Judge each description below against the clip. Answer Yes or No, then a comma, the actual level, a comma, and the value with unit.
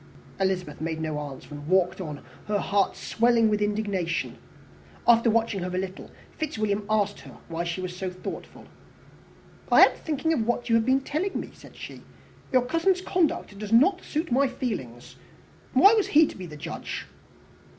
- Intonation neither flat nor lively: No, wide, 6.2 semitones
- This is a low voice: No, high, 210 Hz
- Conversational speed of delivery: Yes, average, 175 wpm